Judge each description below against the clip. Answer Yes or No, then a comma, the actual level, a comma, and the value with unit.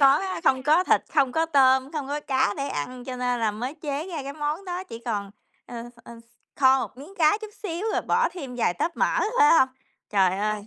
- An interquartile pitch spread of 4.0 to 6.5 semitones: Yes, average, 4.5 semitones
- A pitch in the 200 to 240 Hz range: No, very high, 270 Hz